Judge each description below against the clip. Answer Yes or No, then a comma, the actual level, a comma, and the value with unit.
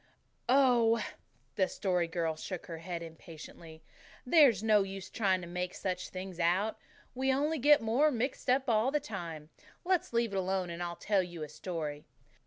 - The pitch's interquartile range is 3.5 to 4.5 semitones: No, wide, 5.6 semitones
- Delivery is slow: No, average, 175 wpm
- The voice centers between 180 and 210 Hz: Yes, high, 190 Hz